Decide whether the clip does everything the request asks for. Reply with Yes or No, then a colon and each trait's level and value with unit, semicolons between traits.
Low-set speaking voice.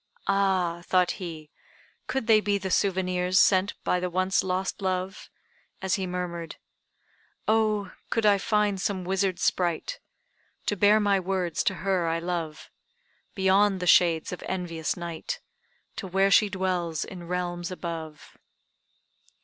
No: medium, 185 Hz